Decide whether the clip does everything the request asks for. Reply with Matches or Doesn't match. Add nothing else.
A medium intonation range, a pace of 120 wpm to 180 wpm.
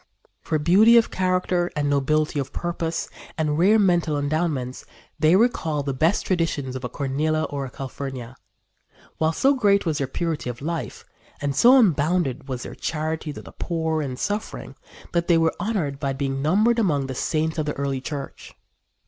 Matches